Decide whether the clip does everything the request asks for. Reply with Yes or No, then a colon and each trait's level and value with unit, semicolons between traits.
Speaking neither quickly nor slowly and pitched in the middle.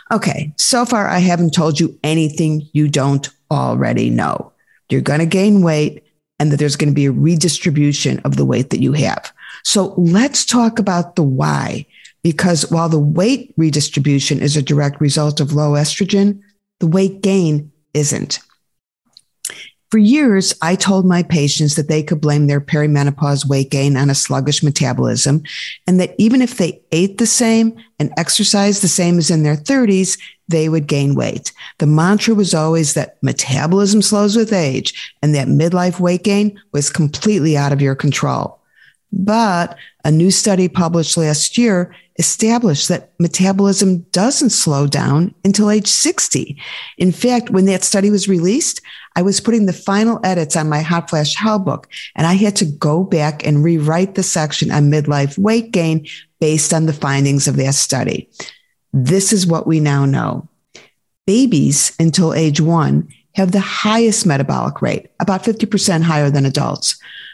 Yes: average, 165 wpm; medium, 165 Hz